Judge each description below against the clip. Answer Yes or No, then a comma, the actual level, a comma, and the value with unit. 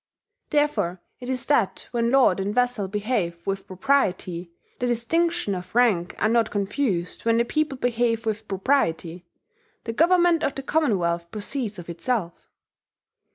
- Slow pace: No, average, 145 wpm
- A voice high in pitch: Yes, high, 225 Hz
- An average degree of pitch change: No, wide, 5.8 semitones